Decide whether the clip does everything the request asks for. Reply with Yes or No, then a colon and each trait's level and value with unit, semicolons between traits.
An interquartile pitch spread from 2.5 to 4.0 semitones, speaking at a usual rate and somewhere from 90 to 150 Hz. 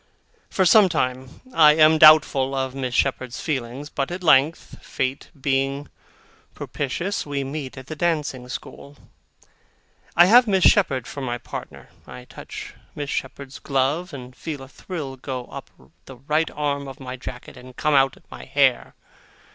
Yes: average, 2.8 semitones; average, 160 wpm; medium, 140 Hz